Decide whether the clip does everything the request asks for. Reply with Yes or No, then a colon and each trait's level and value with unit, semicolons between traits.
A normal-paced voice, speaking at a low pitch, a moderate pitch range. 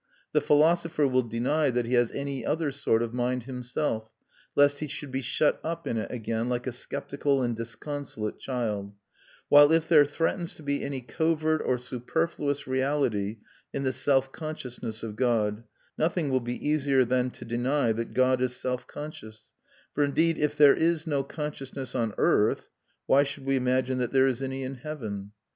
Yes: average, 180 wpm; low, 130 Hz; average, 3.3 semitones